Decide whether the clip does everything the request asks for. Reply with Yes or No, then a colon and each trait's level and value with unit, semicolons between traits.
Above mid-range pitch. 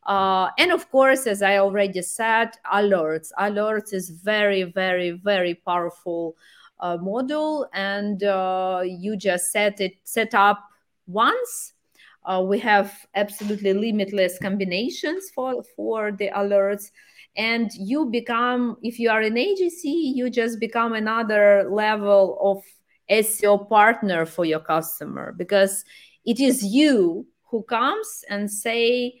Yes: high, 205 Hz